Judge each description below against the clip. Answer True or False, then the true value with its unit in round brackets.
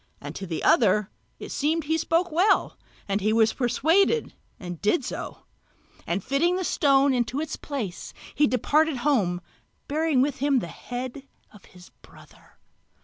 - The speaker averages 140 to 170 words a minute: True (160 wpm)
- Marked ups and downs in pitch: True (6.7 semitones)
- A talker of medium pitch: False (270 Hz)